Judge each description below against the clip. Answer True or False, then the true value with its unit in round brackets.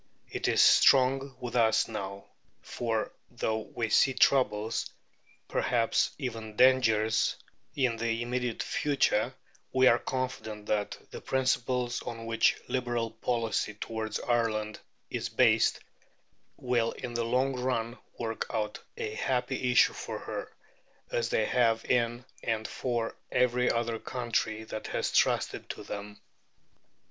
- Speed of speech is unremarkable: False (130 wpm)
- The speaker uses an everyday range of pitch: False (2.2 semitones)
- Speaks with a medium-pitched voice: False (115 Hz)